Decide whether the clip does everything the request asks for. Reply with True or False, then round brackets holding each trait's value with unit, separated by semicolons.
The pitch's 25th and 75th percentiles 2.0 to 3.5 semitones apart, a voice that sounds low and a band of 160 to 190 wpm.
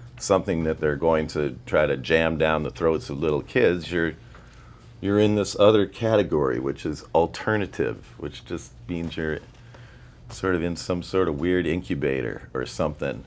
False (4.5 semitones; 90 Hz; 165 wpm)